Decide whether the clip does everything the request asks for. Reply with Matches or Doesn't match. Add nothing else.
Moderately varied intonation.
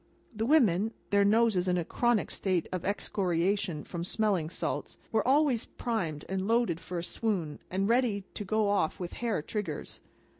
Matches